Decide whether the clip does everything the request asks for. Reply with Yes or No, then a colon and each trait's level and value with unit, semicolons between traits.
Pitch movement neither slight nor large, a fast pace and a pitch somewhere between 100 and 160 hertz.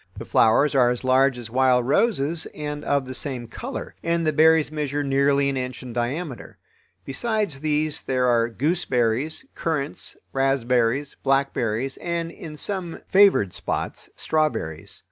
No: average, 3.7 semitones; average, 145 wpm; medium, 140 Hz